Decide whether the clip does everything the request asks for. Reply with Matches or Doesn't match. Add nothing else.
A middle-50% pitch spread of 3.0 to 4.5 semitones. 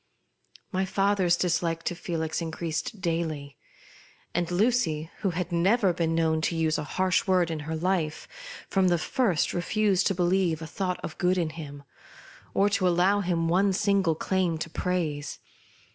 Doesn't match